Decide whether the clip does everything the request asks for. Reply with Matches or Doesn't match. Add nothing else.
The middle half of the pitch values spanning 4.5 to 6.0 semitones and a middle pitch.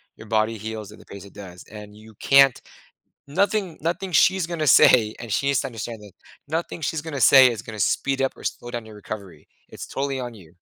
Doesn't match